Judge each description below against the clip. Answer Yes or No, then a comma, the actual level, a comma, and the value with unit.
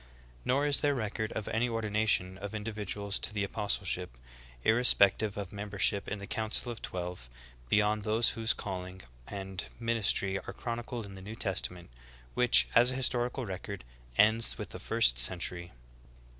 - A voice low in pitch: Yes, low, 105 Hz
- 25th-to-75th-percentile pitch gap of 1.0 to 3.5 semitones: Yes, average, 3.0 semitones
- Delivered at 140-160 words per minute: Yes, average, 155 wpm